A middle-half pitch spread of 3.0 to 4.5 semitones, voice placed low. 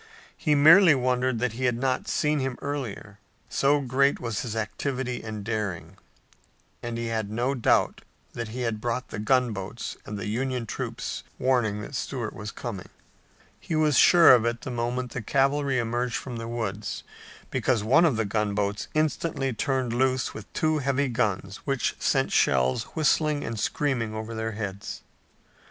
Yes: average, 3.7 semitones; low, 120 Hz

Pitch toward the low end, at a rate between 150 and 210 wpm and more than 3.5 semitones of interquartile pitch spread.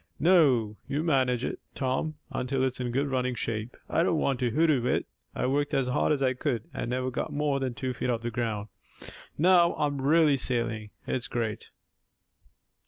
No: low, 130 Hz; average, 185 wpm; average, 3.1 semitones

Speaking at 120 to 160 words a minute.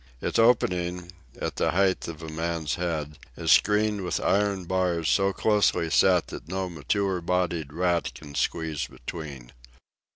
Yes: average, 150 wpm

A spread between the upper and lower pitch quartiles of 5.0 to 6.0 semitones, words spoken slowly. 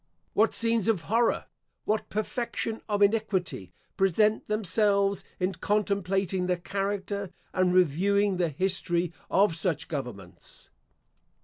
No: average, 2.7 semitones; slow, 110 wpm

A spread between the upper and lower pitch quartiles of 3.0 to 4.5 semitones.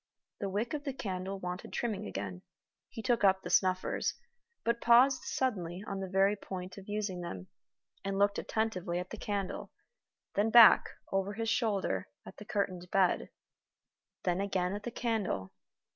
Yes: average, 3.3 semitones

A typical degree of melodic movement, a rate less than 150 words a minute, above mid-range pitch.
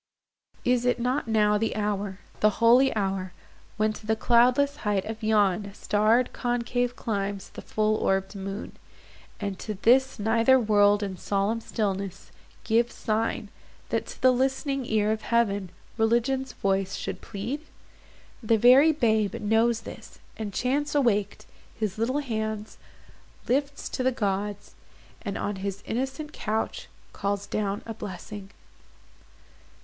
Yes: average, 3.1 semitones; slow, 135 wpm; high, 220 Hz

